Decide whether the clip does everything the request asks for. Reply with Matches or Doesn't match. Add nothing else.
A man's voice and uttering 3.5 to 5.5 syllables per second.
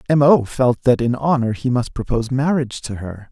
Matches